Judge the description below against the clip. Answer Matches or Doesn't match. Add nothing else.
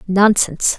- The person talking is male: Doesn't match